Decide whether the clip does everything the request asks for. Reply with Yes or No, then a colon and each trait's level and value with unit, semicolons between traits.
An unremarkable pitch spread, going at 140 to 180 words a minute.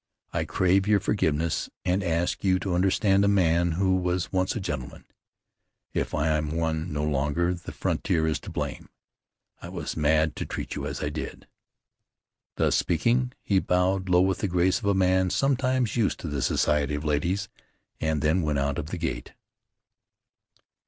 Yes: average, 3.7 semitones; average, 175 wpm